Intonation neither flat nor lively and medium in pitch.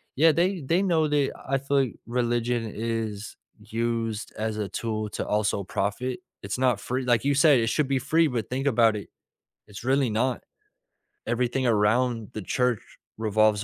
No: average, 3.7 semitones; low, 120 Hz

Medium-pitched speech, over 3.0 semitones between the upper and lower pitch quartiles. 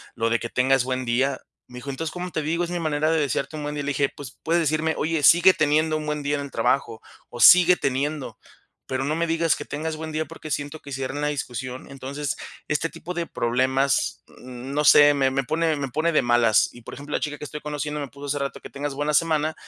No: medium, 145 Hz; average, 2.7 semitones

